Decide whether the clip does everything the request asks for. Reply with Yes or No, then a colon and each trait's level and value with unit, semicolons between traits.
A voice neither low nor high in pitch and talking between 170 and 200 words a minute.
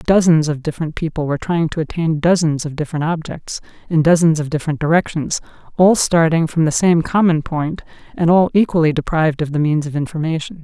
Yes: medium, 160 Hz; average, 185 wpm